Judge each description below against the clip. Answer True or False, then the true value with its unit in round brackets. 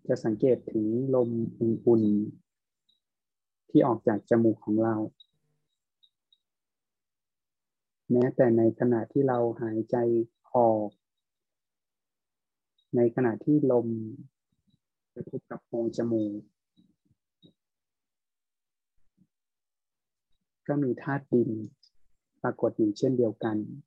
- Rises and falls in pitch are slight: True (2.3 semitones)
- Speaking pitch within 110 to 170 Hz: True (115 Hz)